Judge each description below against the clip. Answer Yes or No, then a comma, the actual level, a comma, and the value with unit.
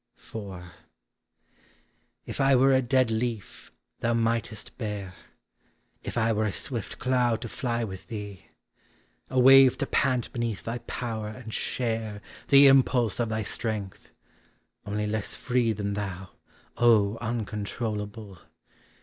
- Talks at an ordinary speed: No, slow, 130 wpm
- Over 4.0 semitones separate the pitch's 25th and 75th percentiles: No, average, 2.8 semitones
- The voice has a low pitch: Yes, low, 115 Hz